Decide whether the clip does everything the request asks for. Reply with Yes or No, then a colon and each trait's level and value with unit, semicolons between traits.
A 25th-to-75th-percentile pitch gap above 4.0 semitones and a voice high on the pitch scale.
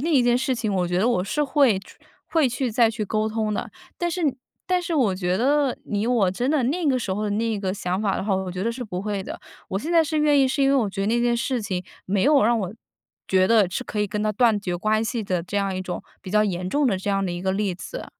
Yes: average, 5.0 semitones; high, 215 Hz